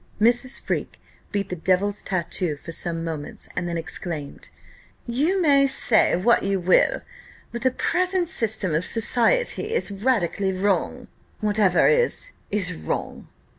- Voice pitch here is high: Yes, high, 205 Hz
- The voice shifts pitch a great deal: Yes, wide, 6.4 semitones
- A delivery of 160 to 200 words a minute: No, slow, 135 wpm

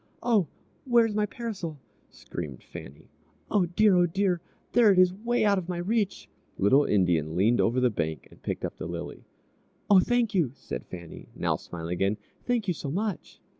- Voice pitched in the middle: Yes, medium, 180 Hz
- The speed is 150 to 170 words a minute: No, average, 180 wpm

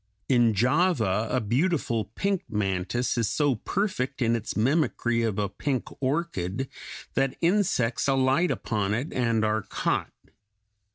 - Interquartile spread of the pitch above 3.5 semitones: Yes, average, 4.7 semitones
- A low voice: Yes, low, 120 Hz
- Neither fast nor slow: No, slow, 130 wpm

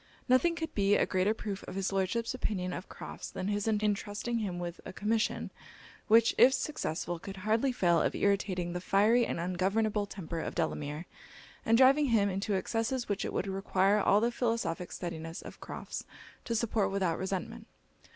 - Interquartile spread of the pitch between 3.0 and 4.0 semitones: Yes, average, 3.6 semitones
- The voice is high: Yes, high, 200 Hz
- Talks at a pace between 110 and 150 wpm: No, average, 175 wpm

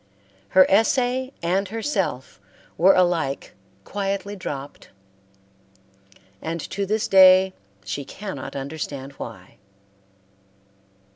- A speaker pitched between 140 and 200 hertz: Yes, medium, 185 Hz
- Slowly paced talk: Yes, slow, 85 wpm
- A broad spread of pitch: Yes, wide, 6.1 semitones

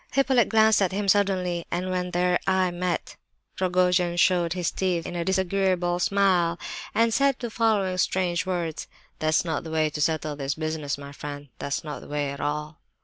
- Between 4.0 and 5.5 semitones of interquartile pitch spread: No, average, 3.2 semitones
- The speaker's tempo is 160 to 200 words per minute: Yes, average, 185 wpm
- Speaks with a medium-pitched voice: Yes, medium, 175 Hz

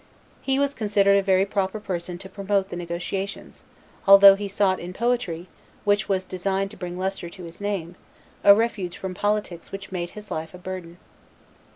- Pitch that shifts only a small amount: Yes, narrow, 2.2 semitones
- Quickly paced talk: No, average, 180 wpm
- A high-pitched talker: Yes, high, 195 Hz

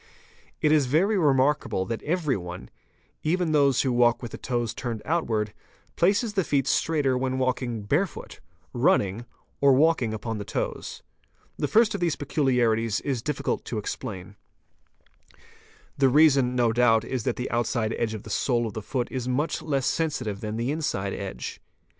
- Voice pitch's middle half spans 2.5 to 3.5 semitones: No, average, 4.7 semitones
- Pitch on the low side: Yes, low, 125 Hz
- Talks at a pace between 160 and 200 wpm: Yes, average, 165 wpm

